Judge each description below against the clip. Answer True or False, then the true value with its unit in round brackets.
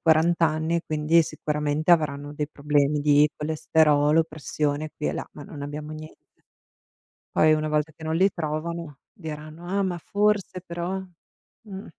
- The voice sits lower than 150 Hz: False (155 Hz)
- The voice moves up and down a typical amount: False (2.0 semitones)